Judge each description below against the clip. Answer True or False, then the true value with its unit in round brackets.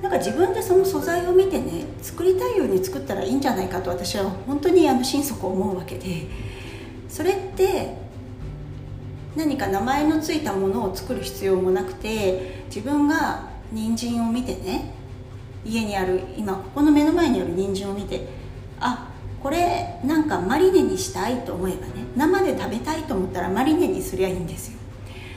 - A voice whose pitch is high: True (235 Hz)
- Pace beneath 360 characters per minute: True (335 characters per minute)